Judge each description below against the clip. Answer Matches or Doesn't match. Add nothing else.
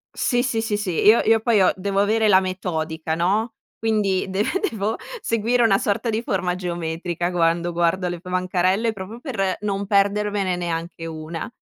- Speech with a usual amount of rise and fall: Matches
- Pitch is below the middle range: Doesn't match